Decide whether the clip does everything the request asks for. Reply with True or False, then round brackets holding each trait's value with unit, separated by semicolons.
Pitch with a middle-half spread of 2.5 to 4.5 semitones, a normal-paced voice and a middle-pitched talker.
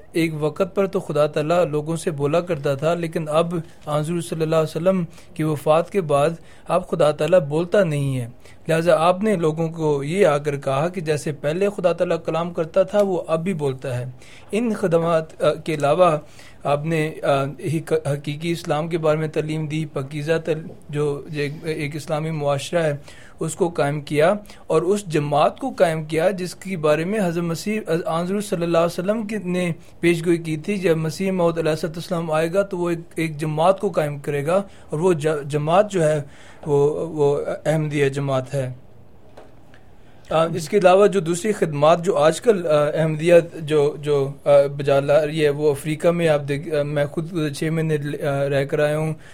True (2.8 semitones; 180 wpm; 160 Hz)